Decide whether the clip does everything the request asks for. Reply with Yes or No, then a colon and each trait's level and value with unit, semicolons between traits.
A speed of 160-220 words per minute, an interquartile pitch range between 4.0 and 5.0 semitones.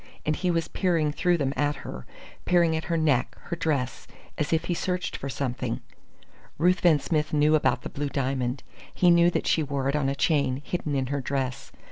No: average, 200 wpm; average, 3.5 semitones